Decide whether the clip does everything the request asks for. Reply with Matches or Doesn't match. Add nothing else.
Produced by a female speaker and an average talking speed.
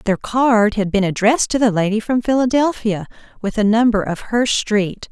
Matches